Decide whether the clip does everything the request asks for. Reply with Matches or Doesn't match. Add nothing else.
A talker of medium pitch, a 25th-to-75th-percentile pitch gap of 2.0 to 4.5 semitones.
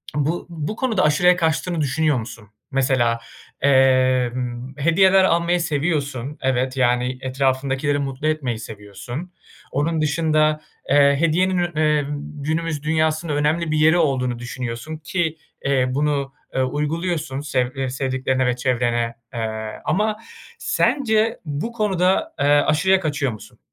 Matches